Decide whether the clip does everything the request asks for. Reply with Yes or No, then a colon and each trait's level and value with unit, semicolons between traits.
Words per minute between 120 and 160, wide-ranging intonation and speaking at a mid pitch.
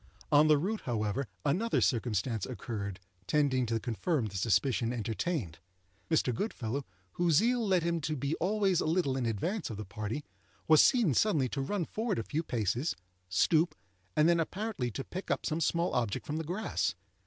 No: average, 175 wpm; wide, 7.1 semitones; medium, 145 Hz